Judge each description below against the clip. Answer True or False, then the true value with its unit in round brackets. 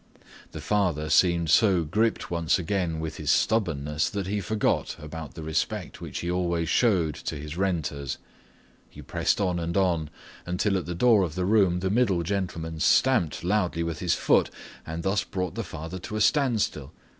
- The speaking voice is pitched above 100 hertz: False (90 Hz)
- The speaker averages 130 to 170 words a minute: False (180 wpm)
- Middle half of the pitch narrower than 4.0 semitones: True (3.4 semitones)